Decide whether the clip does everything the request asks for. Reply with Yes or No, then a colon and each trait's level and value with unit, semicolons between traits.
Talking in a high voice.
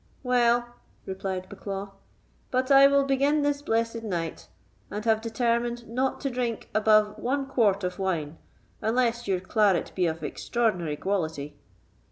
Yes: high, 225 Hz